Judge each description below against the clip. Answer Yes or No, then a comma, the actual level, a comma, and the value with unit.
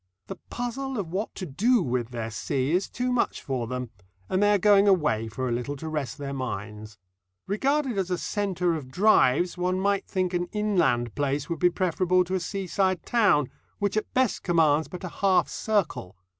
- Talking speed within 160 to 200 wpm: Yes, average, 195 wpm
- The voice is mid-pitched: Yes, medium, 180 Hz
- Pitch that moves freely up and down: Yes, wide, 6.8 semitones